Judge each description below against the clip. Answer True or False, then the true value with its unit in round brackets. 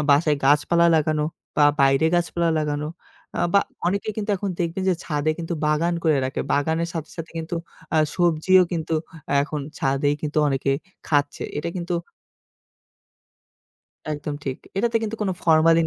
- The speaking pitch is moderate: True (160 Hz)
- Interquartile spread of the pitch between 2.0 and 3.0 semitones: True (2.7 semitones)